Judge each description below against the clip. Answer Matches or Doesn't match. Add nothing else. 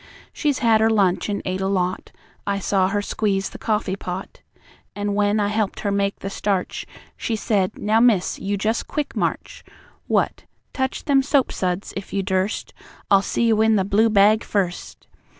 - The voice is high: Matches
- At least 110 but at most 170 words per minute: Doesn't match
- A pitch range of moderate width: Doesn't match